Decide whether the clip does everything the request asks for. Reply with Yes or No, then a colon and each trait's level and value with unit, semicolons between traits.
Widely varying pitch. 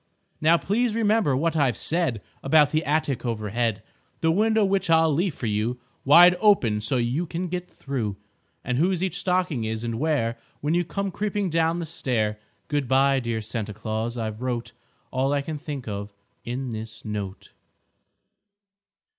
Yes: wide, 6.6 semitones